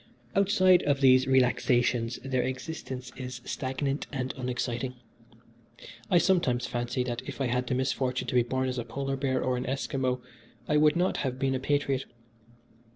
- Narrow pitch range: Yes, narrow, 1.5 semitones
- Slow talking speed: No, average, 160 wpm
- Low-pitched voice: Yes, low, 130 Hz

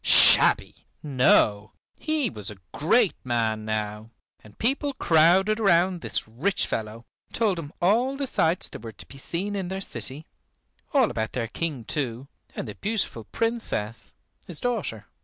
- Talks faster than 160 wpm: No, average, 155 wpm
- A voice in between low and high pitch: Yes, medium, 160 Hz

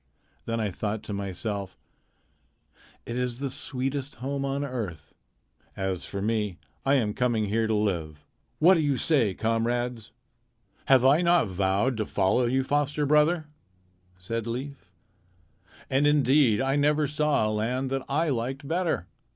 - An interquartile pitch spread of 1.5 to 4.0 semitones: No, average, 4.9 semitones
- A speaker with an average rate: Yes, average, 150 wpm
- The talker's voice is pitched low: Yes, low, 125 Hz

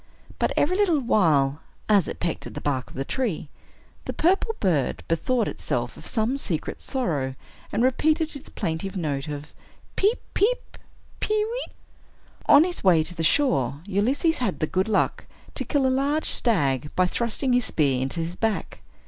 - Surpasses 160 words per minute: Yes, average, 175 wpm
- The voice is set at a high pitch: Yes, high, 205 Hz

